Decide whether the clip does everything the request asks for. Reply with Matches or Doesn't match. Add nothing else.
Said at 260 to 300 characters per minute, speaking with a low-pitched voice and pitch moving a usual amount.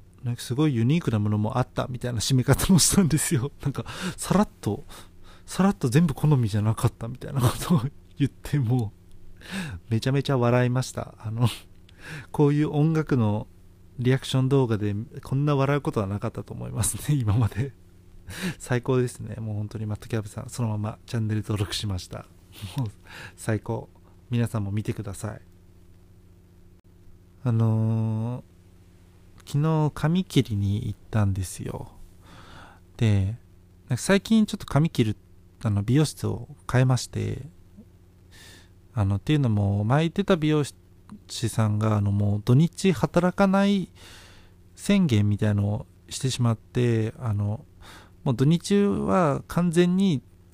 Doesn't match